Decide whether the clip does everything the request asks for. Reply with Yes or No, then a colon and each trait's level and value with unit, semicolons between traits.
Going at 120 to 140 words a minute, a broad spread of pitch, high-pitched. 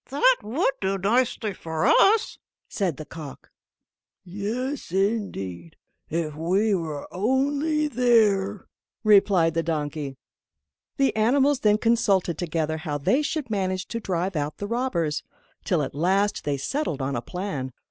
Yes: slow, 135 wpm; wide, 6.6 semitones; high, 195 Hz